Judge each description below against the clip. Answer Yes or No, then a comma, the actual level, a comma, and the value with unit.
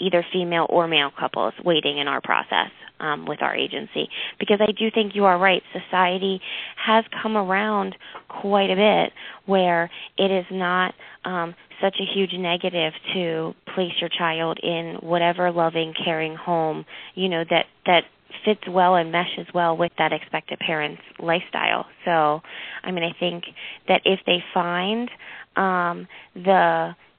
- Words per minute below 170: Yes, average, 155 wpm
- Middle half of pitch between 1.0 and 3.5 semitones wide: Yes, narrow, 2.4 semitones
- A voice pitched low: No, medium, 175 Hz